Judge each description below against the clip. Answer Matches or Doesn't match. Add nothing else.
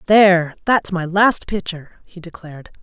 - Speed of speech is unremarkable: Matches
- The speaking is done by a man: Doesn't match